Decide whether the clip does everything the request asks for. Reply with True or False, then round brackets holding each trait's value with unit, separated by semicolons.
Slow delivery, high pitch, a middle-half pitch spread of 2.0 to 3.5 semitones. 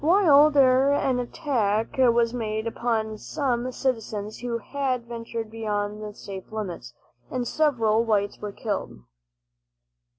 True (125 wpm; 230 Hz; 3.1 semitones)